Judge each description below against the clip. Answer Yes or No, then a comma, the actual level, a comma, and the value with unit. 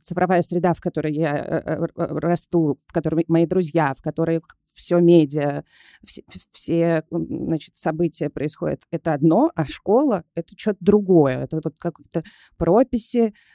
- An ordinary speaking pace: Yes, average, 135 wpm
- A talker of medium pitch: Yes, medium, 170 Hz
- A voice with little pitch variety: Yes, narrow, 1.9 semitones